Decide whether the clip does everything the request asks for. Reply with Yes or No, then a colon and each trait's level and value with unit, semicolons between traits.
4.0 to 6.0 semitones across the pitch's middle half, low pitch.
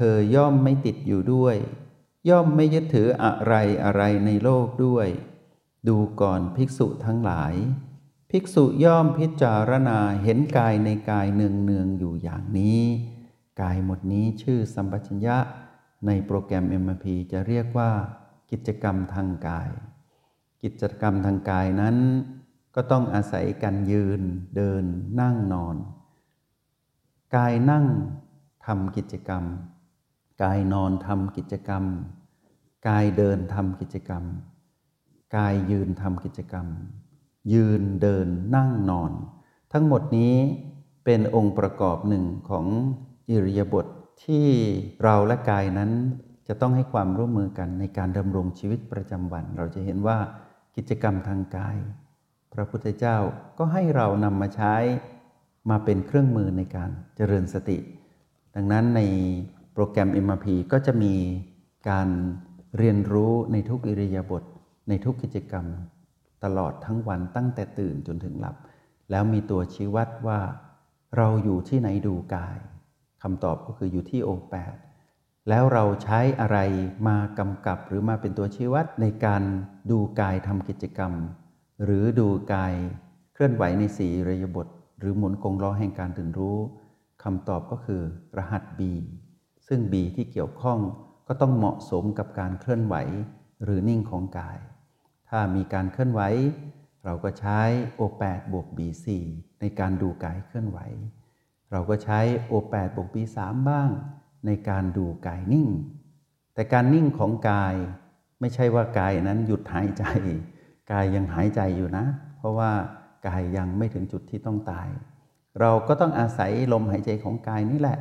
Yes: average, 4.4 semitones; low, 105 Hz